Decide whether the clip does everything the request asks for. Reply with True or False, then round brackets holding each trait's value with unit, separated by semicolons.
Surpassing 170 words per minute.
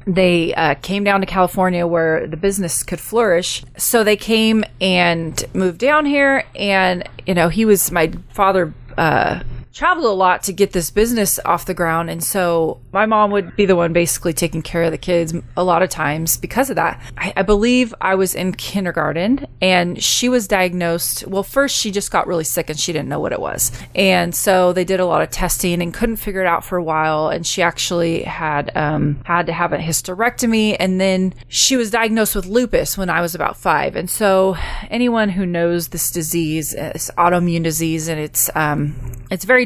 True (205 wpm)